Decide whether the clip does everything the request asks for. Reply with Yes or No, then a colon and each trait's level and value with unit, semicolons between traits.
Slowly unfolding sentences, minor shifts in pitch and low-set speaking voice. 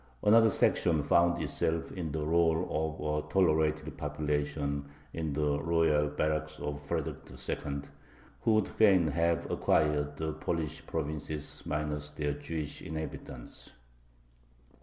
Yes: slow, 120 wpm; narrow, 1.8 semitones; very low, 75 Hz